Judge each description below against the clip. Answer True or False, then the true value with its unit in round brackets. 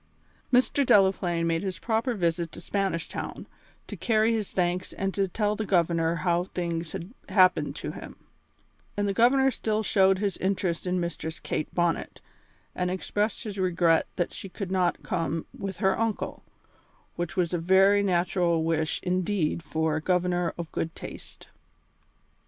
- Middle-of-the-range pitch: True (180 Hz)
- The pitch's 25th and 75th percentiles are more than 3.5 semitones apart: False (2.7 semitones)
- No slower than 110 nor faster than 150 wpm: False (160 wpm)